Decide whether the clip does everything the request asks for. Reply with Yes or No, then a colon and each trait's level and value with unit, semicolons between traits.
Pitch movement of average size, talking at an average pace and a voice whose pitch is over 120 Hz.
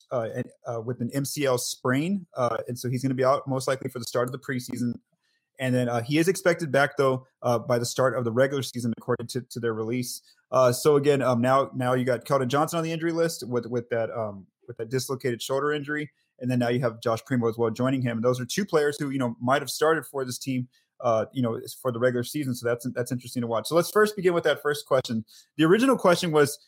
No: average, 3.0 semitones; fast, 265 wpm; low, 130 Hz